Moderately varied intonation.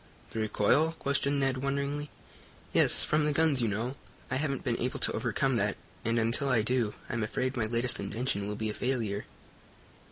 Yes: average, 3.9 semitones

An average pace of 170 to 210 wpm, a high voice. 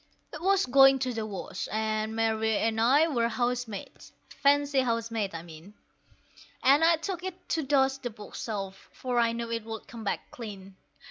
Yes: average, 185 wpm; high, 230 Hz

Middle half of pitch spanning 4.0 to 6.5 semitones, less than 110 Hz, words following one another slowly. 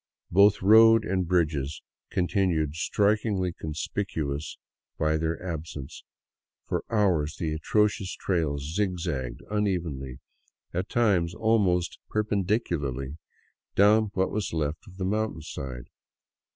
Yes: average, 4.8 semitones; very low, 90 Hz; slow, 105 wpm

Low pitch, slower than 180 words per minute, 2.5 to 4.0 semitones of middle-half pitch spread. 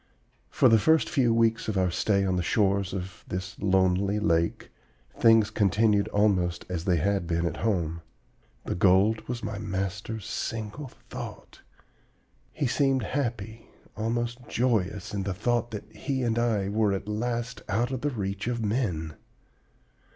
Yes: low, 105 Hz; average, 155 wpm; average, 3.4 semitones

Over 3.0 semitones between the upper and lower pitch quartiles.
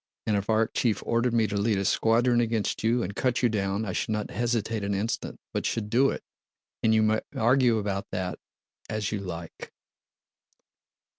No: narrow, 2.4 semitones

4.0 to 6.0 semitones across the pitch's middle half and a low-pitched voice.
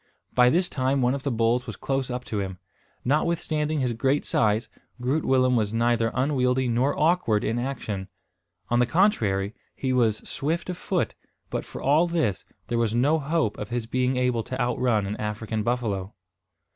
No: average, 3.5 semitones; low, 125 Hz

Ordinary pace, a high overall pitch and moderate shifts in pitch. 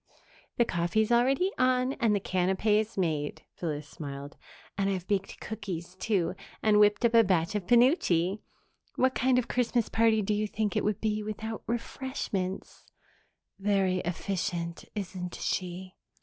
Yes: average, 150 wpm; high, 205 Hz; average, 3.8 semitones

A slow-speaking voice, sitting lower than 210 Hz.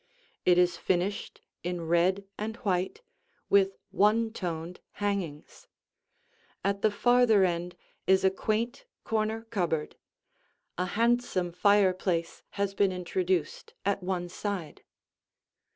Yes: slow, 110 wpm; high, 190 Hz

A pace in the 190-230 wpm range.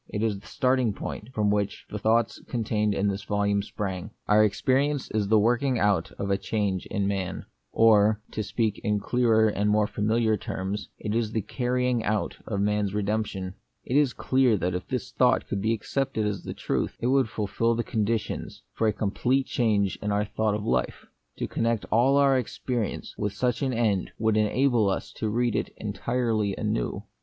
Yes: average, 195 wpm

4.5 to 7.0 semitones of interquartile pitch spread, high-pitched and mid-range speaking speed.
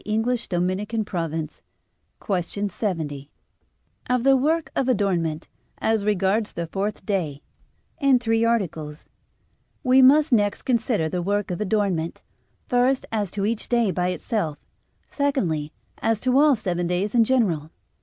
No: average, 5.3 semitones; high, 205 Hz; slow, 130 wpm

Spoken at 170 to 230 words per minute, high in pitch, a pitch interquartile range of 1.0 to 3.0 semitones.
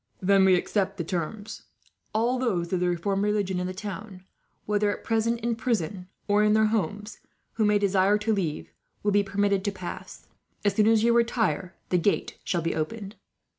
Yes: average, 190 wpm; high, 205 Hz; narrow, 2.6 semitones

